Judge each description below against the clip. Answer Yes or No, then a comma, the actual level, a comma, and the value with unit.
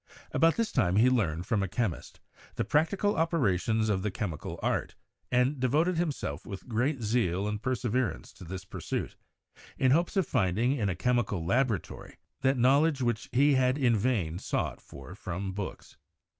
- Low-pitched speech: Yes, low, 120 Hz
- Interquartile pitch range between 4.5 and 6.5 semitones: Yes, wide, 5.5 semitones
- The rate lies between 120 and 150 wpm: No, average, 170 wpm